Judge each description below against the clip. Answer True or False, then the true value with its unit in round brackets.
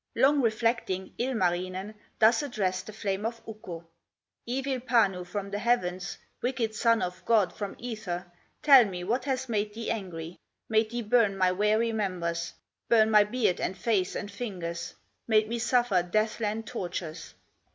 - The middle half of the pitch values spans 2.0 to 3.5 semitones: False (4.0 semitones)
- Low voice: False (215 Hz)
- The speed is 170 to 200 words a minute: False (155 wpm)